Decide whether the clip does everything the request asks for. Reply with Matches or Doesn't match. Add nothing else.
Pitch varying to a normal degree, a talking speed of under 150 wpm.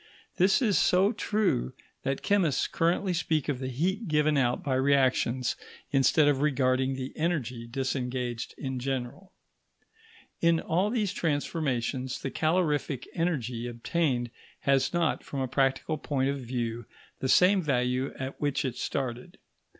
Matches